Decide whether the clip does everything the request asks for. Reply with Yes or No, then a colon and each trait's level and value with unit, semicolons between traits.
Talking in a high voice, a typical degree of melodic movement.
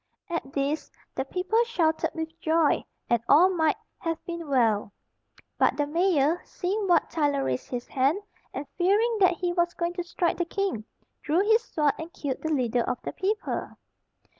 Yes: very high, 330 Hz; average, 4.3 semitones